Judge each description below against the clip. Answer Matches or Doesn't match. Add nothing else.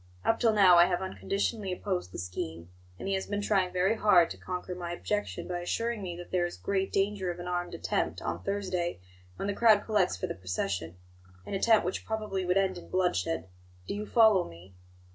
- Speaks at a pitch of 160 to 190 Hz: Matches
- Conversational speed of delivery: Doesn't match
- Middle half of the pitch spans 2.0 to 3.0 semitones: Matches